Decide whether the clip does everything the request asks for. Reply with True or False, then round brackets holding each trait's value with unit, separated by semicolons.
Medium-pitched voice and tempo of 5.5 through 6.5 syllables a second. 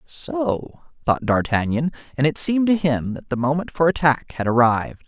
False (145 Hz; 5.0 syllables/s)